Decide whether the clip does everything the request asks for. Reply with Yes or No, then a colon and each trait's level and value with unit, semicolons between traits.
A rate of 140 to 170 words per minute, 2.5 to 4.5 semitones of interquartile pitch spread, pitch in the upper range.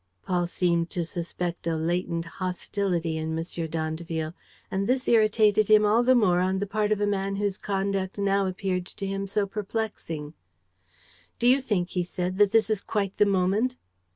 No: average, 180 wpm; average, 3.0 semitones; high, 195 Hz